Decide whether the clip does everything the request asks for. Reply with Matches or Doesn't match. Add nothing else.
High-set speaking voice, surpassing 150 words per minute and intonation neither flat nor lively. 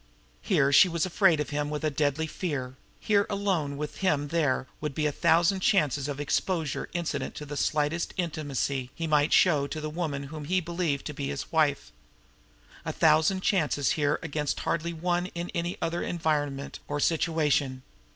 Doesn't match